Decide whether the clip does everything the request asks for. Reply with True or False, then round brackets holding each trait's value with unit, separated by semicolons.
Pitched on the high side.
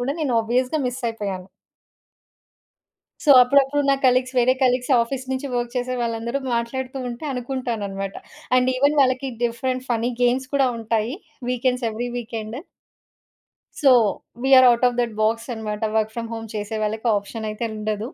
True (240 Hz)